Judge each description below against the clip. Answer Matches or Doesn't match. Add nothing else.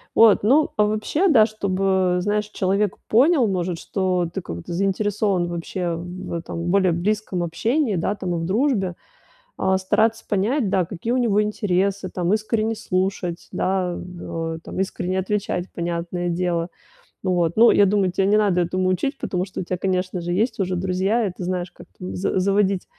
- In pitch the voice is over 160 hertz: Matches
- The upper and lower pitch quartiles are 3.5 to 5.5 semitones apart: Doesn't match